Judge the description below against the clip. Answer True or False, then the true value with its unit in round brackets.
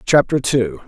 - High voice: False (125 Hz)